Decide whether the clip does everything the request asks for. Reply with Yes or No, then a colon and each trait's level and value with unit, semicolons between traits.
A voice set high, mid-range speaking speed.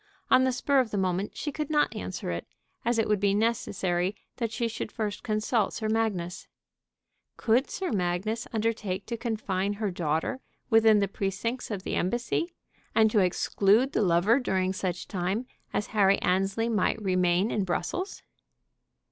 Yes: high, 210 Hz; average, 165 wpm